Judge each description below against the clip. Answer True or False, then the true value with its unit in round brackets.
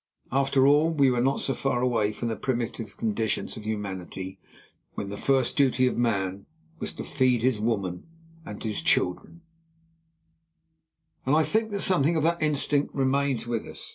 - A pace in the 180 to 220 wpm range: False (170 wpm)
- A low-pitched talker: True (125 Hz)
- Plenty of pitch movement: False (4.6 semitones)